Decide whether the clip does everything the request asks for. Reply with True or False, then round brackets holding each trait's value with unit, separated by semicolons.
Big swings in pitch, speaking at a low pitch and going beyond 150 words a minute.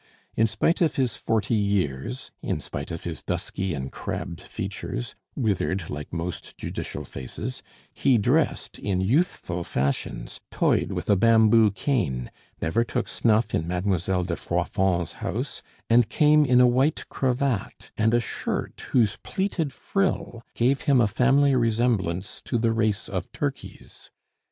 False (5.8 semitones; 110 Hz; 145 wpm)